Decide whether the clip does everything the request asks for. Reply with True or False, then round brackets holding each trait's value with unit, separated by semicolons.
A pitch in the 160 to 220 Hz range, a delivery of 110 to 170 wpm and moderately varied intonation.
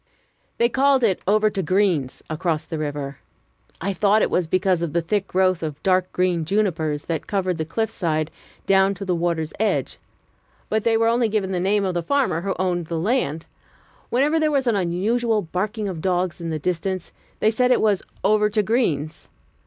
False (190 Hz; 195 wpm; 4.3 semitones)